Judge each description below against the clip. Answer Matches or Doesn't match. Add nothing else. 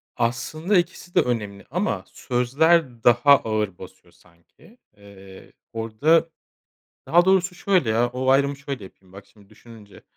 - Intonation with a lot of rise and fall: Matches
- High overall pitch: Doesn't match